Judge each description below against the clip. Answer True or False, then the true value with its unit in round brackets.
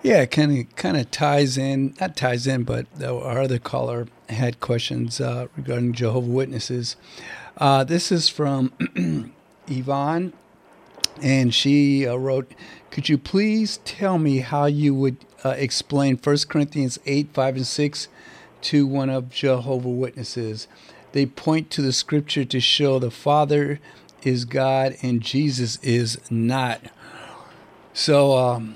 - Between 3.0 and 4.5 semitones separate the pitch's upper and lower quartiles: False (2.6 semitones)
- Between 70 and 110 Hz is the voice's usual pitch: False (135 Hz)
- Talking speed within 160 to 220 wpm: False (140 wpm)